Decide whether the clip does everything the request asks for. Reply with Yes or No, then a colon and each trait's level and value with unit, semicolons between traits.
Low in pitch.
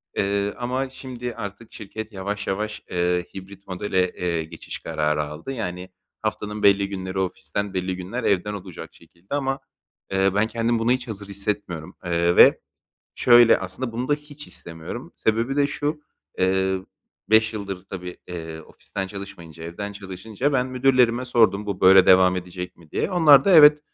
Yes: low, 100 Hz